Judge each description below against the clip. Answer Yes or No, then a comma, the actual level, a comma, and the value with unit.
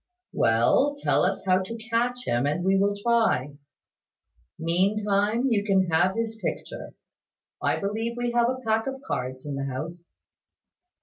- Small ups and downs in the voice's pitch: No, wide, 5.5 semitones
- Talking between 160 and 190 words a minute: No, average, 150 wpm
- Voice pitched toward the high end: Yes, high, 200 Hz